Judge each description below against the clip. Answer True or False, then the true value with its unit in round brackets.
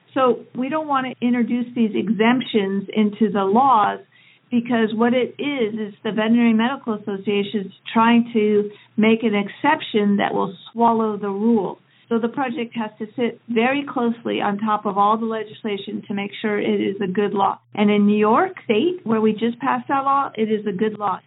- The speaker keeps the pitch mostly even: True (2.2 semitones)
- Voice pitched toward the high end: True (220 Hz)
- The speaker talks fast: False (195 wpm)